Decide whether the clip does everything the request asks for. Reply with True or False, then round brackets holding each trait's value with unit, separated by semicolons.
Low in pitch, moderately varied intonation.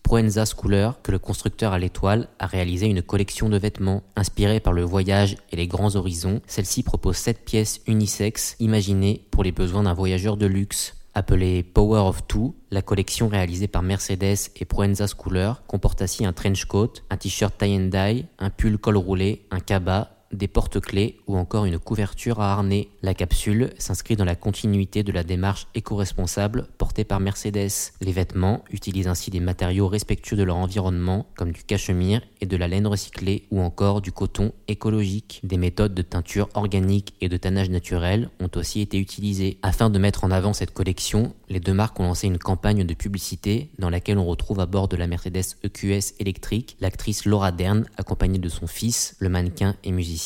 False (100 Hz; 2.0 semitones)